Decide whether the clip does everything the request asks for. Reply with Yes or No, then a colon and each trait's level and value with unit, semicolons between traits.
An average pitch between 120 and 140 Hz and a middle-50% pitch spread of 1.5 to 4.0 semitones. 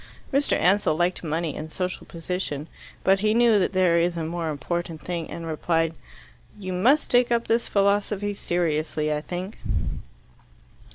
No: medium, 175 Hz; average, 3.7 semitones